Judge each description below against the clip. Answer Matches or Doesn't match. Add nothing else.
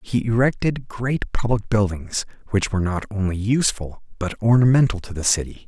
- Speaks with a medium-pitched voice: Doesn't match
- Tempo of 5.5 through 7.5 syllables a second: Doesn't match